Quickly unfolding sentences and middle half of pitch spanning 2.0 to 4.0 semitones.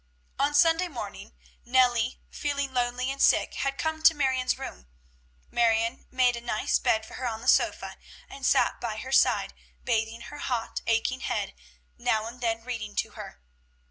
No: average, 170 wpm; average, 3.1 semitones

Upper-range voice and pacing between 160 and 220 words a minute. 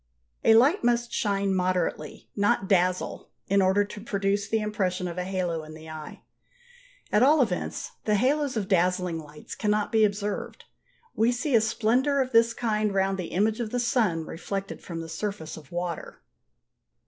Yes: high, 200 Hz; average, 170 wpm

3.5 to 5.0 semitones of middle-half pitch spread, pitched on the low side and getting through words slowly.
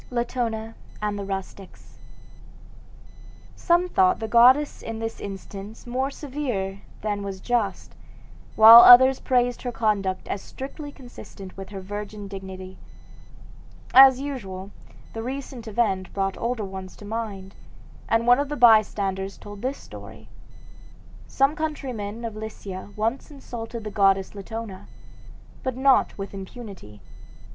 No: average, 4.1 semitones; high, 220 Hz; slow, 130 wpm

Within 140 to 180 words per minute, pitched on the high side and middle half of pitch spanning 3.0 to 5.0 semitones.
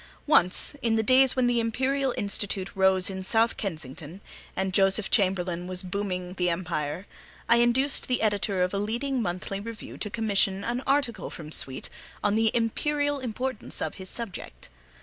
Yes: average, 165 wpm; high, 205 Hz; average, 4.4 semitones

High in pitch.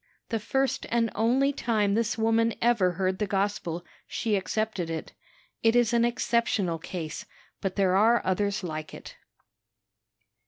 Yes: high, 210 Hz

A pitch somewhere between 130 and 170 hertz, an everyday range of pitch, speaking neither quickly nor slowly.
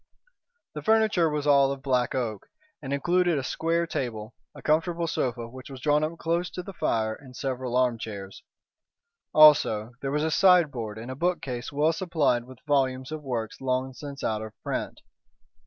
Yes: low, 135 Hz; average, 4.5 semitones; average, 175 wpm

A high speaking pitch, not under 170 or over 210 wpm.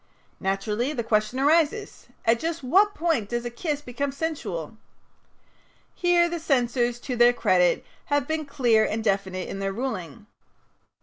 No: high, 245 Hz; average, 145 wpm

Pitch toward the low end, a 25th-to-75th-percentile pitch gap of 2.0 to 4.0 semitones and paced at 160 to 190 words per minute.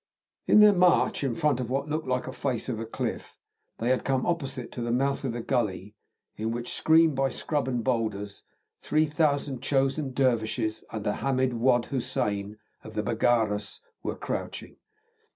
Yes: low, 130 Hz; average, 3.4 semitones; average, 165 wpm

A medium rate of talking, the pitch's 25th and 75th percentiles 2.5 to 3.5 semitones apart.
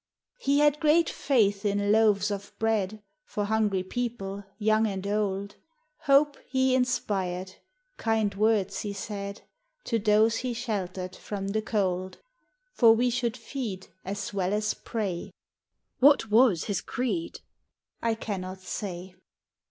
No: slow, 130 wpm; average, 3.0 semitones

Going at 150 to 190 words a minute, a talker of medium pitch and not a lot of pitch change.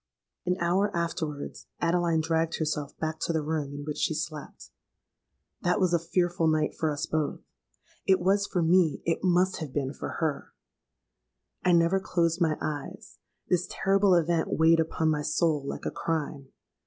Yes: average, 165 wpm; medium, 165 Hz; narrow, 2.3 semitones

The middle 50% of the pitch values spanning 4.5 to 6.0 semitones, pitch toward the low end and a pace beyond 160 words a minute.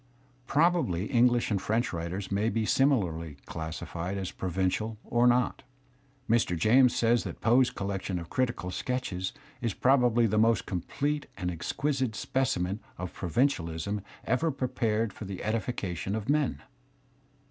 No: average, 5.3 semitones; low, 110 Hz; average, 145 wpm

